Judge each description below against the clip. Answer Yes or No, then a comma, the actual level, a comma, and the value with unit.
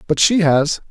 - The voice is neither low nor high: Yes, medium, 165 Hz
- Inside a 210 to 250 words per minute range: No, average, 200 wpm